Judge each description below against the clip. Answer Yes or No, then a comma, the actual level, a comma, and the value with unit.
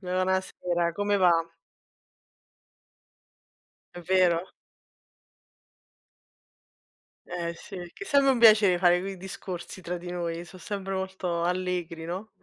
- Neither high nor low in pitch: Yes, medium, 180 Hz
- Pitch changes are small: Yes, narrow, 1.7 semitones